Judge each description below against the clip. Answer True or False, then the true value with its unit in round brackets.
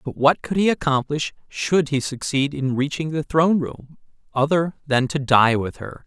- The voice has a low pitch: False (145 Hz)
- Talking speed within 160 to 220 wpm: True (190 wpm)